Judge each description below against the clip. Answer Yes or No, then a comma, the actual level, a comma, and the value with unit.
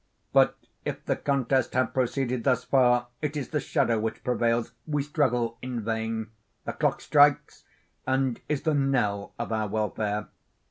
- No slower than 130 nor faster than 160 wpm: Yes, average, 150 wpm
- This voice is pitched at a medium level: No, low, 125 Hz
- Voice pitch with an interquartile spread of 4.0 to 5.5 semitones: No, average, 3.4 semitones